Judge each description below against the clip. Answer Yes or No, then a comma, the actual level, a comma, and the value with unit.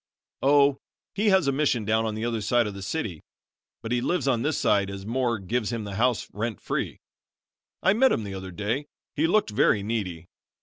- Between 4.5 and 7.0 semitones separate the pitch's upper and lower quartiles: Yes, average, 5.1 semitones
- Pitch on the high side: No, low, 115 Hz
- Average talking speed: No, fast, 210 wpm